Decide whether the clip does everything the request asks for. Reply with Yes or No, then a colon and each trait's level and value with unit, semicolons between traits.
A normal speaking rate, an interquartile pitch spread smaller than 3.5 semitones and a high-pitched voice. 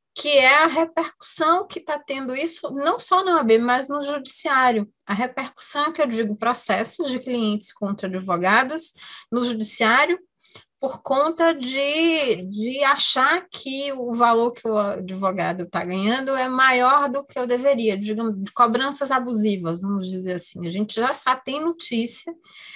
No: average, 155 wpm; average, 4.9 semitones; very high, 255 Hz